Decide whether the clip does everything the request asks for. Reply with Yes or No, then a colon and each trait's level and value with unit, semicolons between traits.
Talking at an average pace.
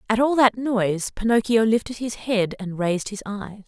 Yes: average, 195 wpm